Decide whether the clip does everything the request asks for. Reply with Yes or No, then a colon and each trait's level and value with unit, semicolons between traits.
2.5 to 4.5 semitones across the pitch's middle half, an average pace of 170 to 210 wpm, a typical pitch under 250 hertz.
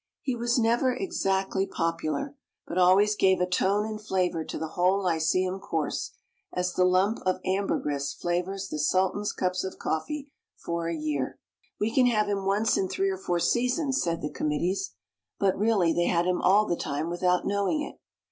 Yes: average, 3.3 semitones; average, 180 wpm; high, 190 Hz